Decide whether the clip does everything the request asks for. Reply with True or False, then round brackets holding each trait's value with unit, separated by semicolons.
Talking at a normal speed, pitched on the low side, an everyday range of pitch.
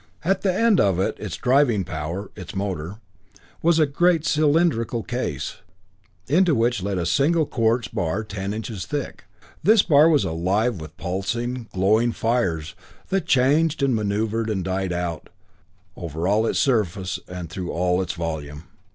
False (155 wpm; 110 Hz; 7.3 semitones)